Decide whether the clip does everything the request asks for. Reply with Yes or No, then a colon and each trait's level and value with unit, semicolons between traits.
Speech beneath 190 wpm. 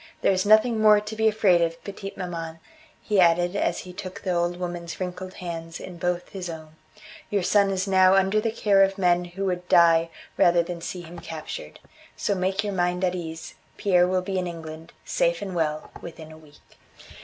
No: average, 200 wpm